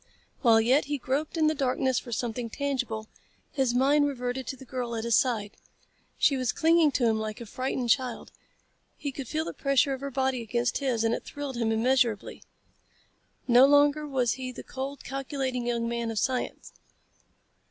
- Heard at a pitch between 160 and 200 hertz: No, very high, 255 Hz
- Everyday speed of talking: Yes, average, 185 wpm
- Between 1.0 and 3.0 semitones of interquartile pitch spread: Yes, average, 2.7 semitones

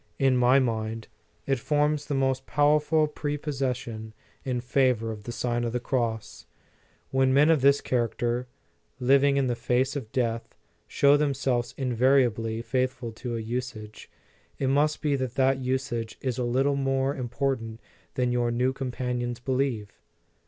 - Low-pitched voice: Yes, low, 130 Hz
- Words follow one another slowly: No, average, 150 wpm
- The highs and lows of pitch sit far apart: No, narrow, 2.4 semitones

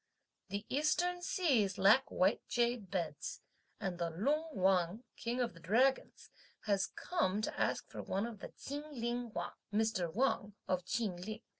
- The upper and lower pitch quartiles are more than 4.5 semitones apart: Yes, average, 5.1 semitones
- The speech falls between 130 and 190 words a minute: Yes, average, 160 wpm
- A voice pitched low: No, high, 220 Hz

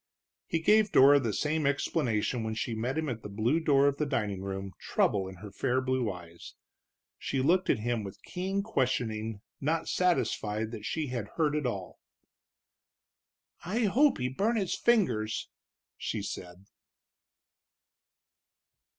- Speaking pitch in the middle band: No, low, 125 Hz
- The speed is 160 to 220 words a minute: No, average, 150 wpm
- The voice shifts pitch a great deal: Yes, wide, 6.9 semitones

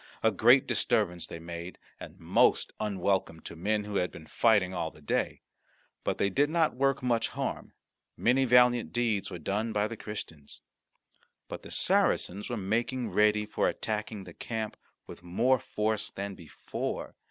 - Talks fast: No, average, 165 wpm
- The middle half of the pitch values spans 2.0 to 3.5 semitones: No, average, 4.3 semitones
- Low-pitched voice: Yes, low, 105 Hz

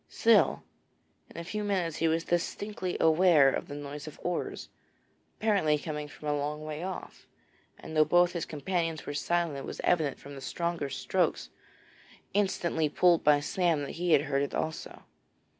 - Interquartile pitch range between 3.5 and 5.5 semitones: No, average, 3.1 semitones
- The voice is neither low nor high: Yes, medium, 160 Hz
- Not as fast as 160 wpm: No, average, 175 wpm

